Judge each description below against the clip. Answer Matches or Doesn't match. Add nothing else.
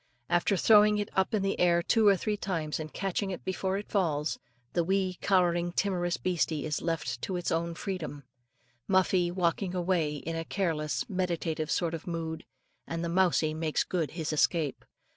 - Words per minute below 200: Matches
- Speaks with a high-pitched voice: Doesn't match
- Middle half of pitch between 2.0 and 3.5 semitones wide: Matches